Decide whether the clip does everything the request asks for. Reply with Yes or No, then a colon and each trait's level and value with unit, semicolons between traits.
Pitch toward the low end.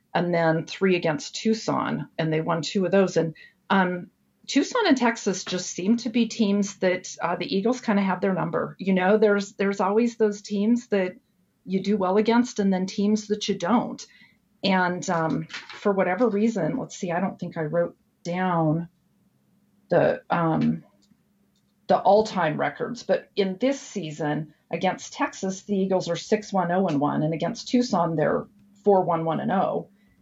No: high, 195 Hz